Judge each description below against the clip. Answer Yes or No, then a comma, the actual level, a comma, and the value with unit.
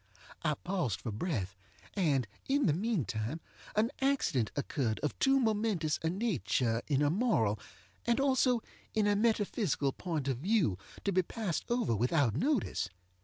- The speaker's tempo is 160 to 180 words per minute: No, average, 150 wpm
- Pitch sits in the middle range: Yes, medium, 170 Hz